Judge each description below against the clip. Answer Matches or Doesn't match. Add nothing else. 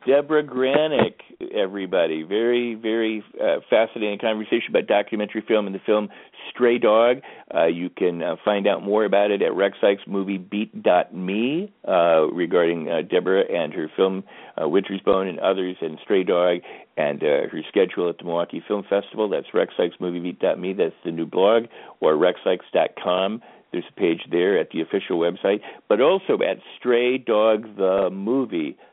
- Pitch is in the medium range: Doesn't match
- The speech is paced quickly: Doesn't match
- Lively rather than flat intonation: Doesn't match